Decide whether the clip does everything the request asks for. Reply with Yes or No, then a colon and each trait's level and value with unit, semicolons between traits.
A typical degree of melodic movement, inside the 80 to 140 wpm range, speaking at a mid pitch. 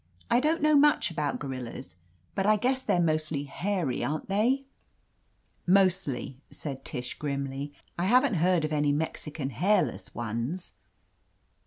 No: wide, 6.5 semitones; slow, 135 wpm; medium, 160 Hz